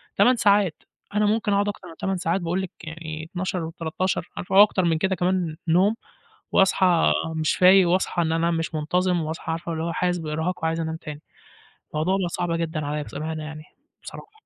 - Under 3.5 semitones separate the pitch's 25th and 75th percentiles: Yes, average, 2.8 semitones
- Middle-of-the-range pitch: Yes, medium, 170 Hz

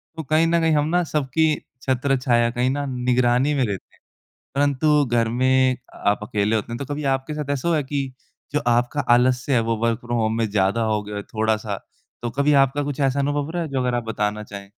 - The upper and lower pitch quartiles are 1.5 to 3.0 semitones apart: No, average, 3.8 semitones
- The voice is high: No, low, 130 Hz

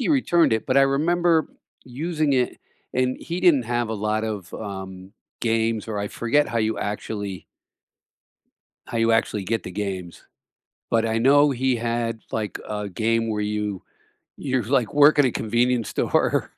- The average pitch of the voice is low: Yes, low, 115 Hz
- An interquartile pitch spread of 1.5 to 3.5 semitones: No, average, 3.9 semitones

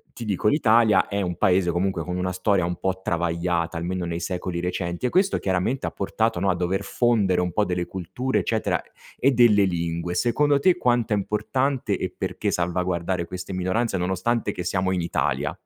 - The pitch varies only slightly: No, average, 4.1 semitones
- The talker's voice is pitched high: No, very low, 95 Hz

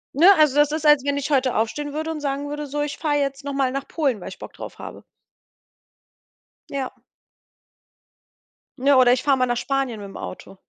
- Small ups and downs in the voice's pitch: Yes, narrow, 2.3 semitones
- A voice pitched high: Yes, very high, 280 Hz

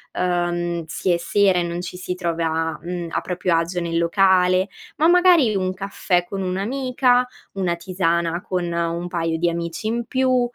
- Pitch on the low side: No, medium, 180 Hz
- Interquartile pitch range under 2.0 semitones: No, narrow, 2.5 semitones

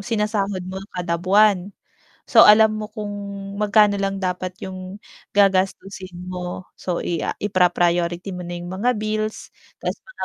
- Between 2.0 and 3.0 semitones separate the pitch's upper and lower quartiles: Yes, average, 2.7 semitones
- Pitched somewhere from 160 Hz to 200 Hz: Yes, high, 190 Hz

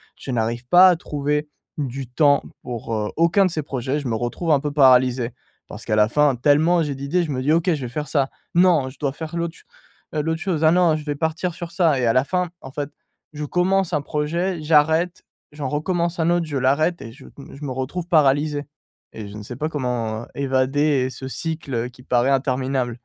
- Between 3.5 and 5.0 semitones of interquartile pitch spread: Yes, average, 3.8 semitones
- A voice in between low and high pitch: Yes, medium, 145 Hz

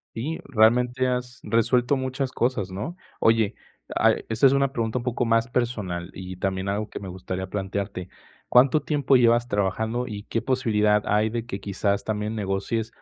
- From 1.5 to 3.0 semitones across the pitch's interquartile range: No, average, 3.6 semitones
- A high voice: No, low, 115 Hz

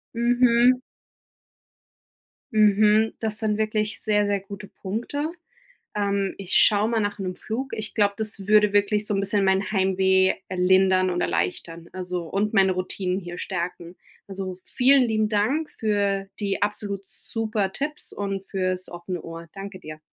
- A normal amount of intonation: No, narrow, 2.3 semitones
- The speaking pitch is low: No, high, 200 Hz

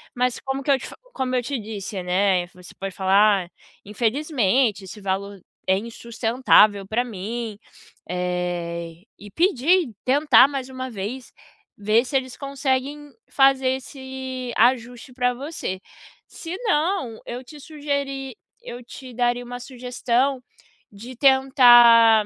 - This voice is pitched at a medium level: No, high, 245 Hz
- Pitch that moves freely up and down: No, average, 4.2 semitones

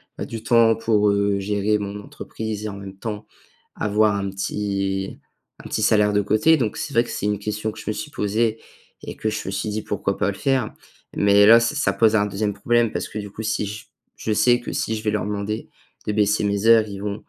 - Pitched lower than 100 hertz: No, low, 105 Hz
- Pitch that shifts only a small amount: Yes, narrow, 1.5 semitones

